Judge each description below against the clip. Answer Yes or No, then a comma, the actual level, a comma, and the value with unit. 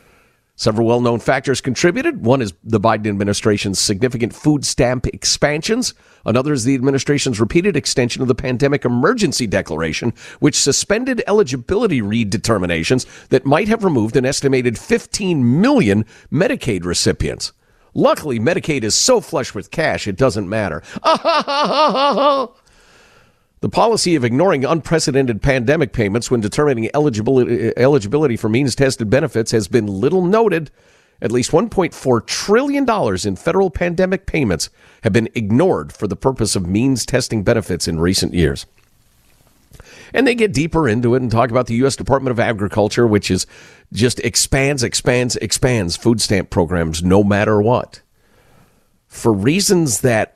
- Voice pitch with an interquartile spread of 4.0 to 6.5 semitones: Yes, average, 5.3 semitones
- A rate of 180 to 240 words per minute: No, average, 140 wpm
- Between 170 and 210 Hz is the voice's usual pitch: No, low, 125 Hz